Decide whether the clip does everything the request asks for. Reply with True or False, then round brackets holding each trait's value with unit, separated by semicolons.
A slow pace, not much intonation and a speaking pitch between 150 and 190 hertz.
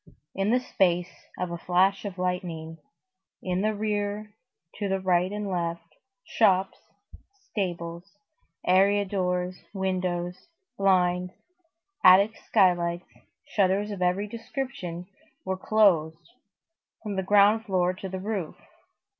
True (115 wpm; 2.3 semitones; 185 Hz)